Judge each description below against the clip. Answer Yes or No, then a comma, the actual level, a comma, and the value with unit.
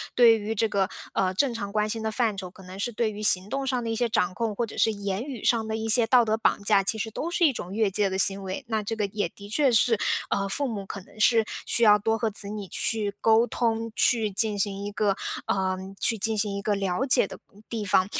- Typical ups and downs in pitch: No, narrow, 2.3 semitones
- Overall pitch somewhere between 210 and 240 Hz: Yes, high, 215 Hz